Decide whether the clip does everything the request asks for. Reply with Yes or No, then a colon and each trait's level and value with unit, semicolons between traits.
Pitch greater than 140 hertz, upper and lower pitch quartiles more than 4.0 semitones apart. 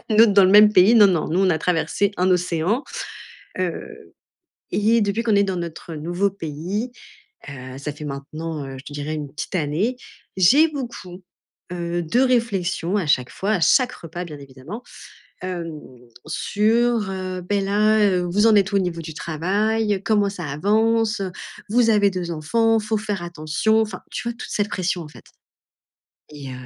Yes: medium, 185 Hz; average, 4.6 semitones